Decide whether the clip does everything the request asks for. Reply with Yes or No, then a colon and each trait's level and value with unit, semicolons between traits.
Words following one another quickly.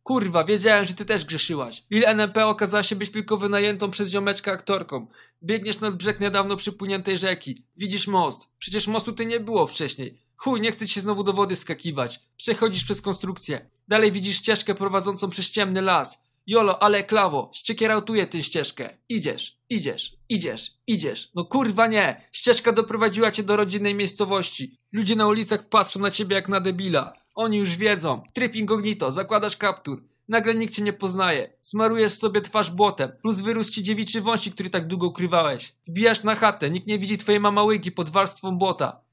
Yes: fast, 170 wpm